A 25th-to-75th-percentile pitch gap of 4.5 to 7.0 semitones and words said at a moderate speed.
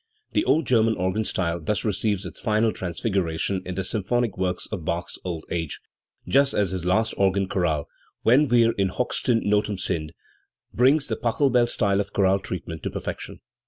No: average, 3.9 semitones; average, 170 wpm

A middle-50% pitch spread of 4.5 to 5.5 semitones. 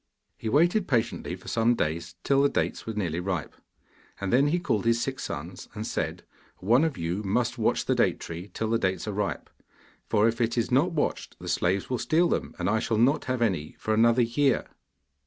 Yes: average, 4.9 semitones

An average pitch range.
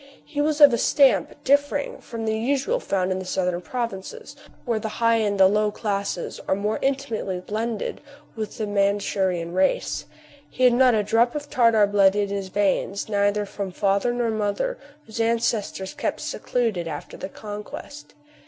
Yes: average, 3.4 semitones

